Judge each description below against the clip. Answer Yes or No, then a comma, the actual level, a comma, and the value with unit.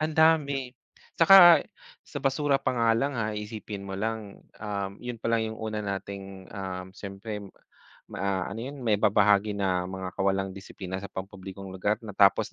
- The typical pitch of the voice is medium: No, low, 105 Hz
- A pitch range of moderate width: Yes, average, 3.1 semitones